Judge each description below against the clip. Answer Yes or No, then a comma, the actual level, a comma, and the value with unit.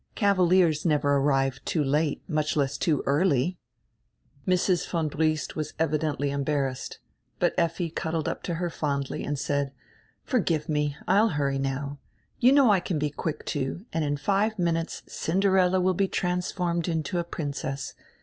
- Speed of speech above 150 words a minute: Yes, average, 160 wpm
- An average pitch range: Yes, average, 3.8 semitones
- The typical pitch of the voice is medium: Yes, medium, 160 Hz